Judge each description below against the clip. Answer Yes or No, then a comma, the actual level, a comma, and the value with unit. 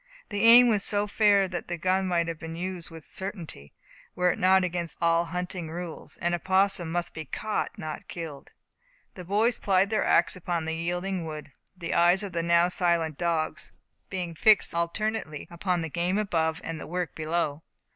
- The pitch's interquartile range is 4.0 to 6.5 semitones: No, narrow, 2.4 semitones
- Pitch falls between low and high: Yes, medium, 175 Hz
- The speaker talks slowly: No, average, 185 wpm